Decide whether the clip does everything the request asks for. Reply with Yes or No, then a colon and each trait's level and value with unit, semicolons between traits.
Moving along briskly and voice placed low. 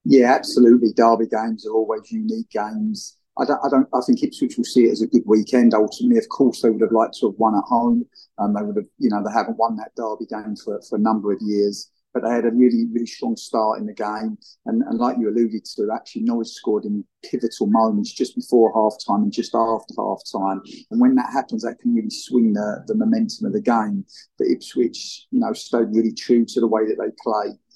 Yes: fast, 240 wpm; low, 115 Hz